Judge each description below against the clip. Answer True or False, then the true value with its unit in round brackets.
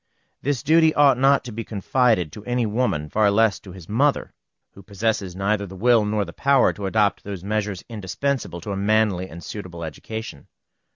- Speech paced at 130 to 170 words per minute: False (185 wpm)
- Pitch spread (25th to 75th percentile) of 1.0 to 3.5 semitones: False (3.9 semitones)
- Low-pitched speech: True (105 Hz)